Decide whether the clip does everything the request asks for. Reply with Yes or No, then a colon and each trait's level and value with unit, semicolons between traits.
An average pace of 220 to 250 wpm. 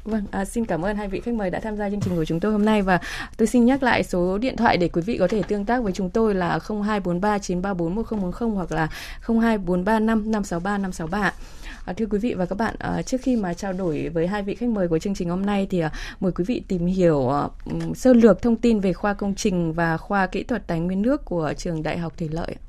Yes: average, 245 wpm